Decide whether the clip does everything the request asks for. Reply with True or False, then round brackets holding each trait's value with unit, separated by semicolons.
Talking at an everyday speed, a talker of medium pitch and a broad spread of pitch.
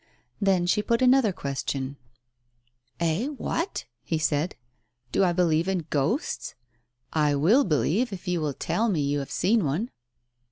True (155 wpm; 175 Hz; 6.3 semitones)